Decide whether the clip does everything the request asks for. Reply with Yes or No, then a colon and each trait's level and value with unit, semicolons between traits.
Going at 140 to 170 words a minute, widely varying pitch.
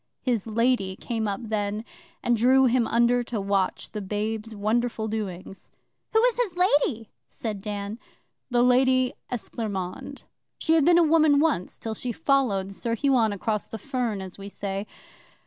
No: average, 160 wpm; average, 4.0 semitones